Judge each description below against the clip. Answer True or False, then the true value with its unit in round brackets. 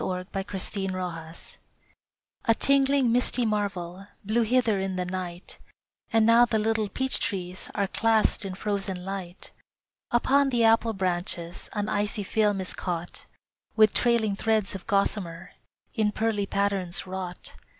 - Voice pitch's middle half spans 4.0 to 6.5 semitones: False (3.3 semitones)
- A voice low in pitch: False (200 Hz)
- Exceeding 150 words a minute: False (135 wpm)